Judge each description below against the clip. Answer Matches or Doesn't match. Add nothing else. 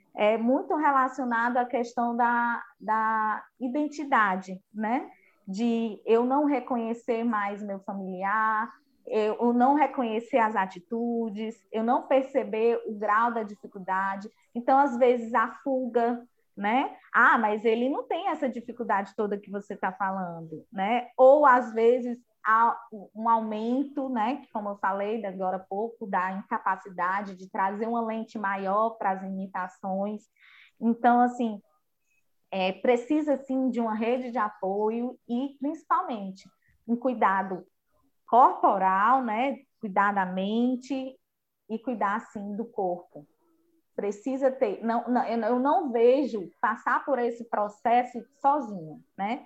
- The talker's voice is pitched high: Matches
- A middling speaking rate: Matches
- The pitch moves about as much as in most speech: Matches